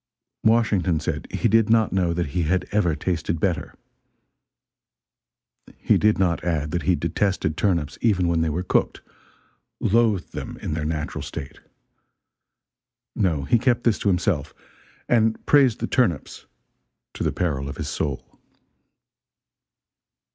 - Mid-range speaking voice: No, very low, 90 Hz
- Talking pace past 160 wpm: No, average, 140 wpm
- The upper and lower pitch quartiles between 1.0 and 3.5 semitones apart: No, average, 5.0 semitones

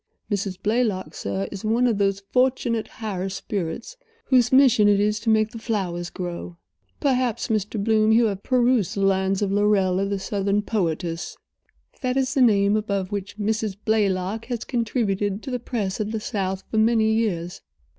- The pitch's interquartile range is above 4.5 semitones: No, average, 2.9 semitones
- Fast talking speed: No, average, 170 wpm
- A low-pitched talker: No, high, 210 Hz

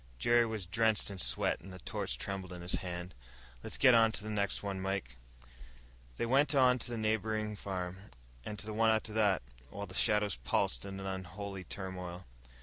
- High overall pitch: No, low, 100 Hz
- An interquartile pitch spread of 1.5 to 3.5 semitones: Yes, average, 3.0 semitones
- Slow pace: No, average, 195 wpm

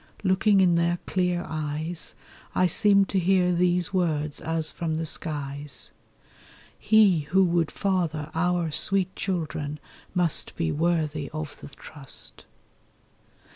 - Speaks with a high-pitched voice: No, medium, 170 Hz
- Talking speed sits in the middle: No, slow, 125 wpm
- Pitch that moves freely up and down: No, average, 3.0 semitones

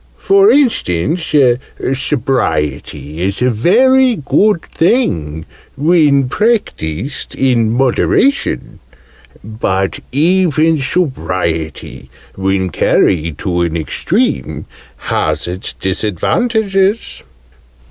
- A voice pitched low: Yes, low, 130 Hz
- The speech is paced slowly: Yes, slow, 75 wpm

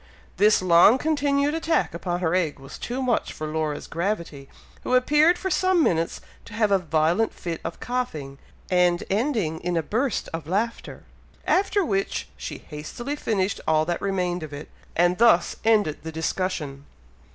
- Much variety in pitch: Yes, wide, 7.1 semitones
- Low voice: No, medium, 185 Hz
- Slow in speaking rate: No, average, 165 wpm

